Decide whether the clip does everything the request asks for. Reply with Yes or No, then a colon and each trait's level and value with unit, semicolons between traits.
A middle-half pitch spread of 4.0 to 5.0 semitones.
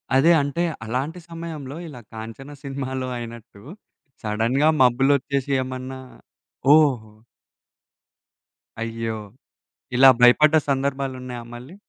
No: average, 2.8 semitones